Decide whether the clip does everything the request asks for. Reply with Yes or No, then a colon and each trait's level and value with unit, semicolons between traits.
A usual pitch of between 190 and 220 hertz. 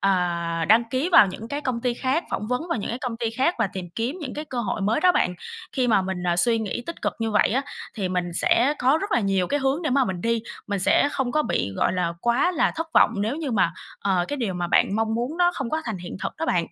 No: high, 230 Hz